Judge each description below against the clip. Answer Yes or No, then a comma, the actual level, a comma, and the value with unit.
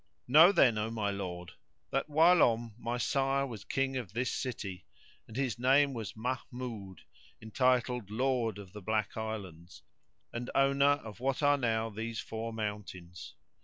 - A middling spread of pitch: Yes, average, 4.0 semitones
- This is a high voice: No, low, 115 Hz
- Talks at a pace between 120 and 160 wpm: Yes, average, 150 wpm